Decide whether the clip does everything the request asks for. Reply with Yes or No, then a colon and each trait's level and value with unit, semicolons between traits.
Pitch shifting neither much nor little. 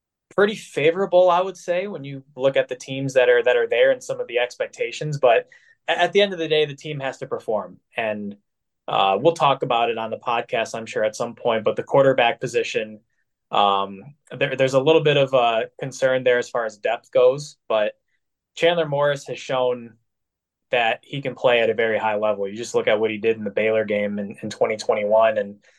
No: wide, 7.3 semitones